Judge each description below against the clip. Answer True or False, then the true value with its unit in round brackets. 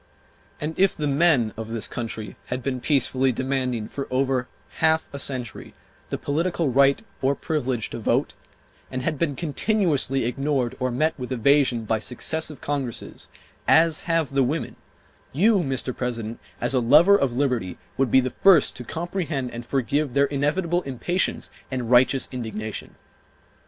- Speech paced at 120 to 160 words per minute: True (155 wpm)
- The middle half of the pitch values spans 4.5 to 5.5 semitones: False (3.8 semitones)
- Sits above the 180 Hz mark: False (135 Hz)